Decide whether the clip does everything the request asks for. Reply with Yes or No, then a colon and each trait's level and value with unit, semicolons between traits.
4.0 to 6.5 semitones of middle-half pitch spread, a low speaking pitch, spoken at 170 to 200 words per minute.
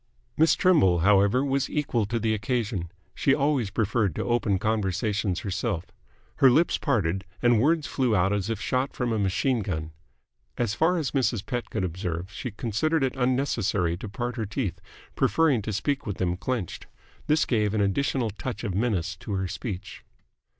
Yes: average, 5.0 semitones; low, 110 Hz; average, 175 wpm